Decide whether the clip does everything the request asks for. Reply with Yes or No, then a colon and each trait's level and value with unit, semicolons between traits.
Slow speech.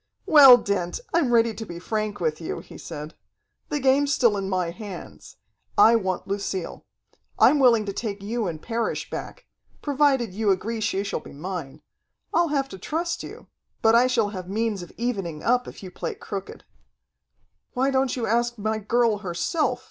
No: average, 180 wpm